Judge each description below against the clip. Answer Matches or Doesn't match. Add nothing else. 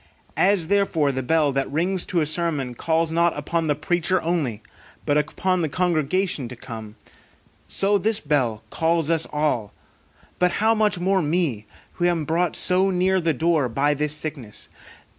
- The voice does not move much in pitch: Doesn't match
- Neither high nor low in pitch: Matches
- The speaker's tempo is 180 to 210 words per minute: Doesn't match